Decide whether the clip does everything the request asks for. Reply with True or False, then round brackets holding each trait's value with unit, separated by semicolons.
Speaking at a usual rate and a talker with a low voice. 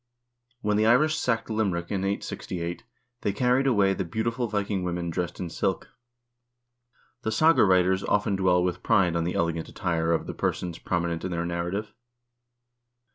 True (170 wpm; 95 Hz)